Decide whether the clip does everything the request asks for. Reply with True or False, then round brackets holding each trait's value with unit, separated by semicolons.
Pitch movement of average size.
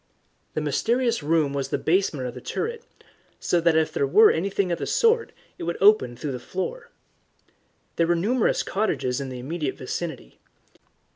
False (7.0 semitones)